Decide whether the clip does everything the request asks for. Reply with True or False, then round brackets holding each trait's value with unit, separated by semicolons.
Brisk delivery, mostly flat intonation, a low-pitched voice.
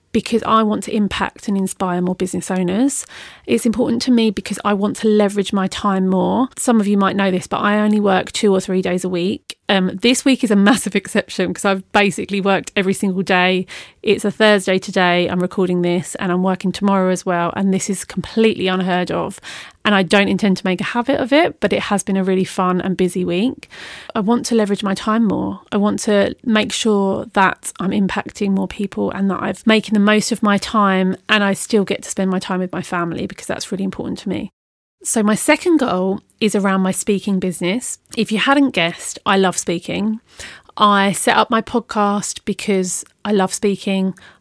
False (215 wpm; 2.3 semitones; 200 Hz)